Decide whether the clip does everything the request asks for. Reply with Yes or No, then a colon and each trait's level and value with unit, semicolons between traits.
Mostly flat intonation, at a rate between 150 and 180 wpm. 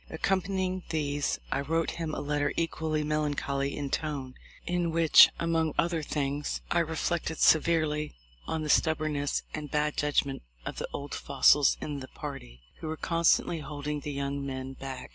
Yes: narrow, 2.3 semitones; average, 165 wpm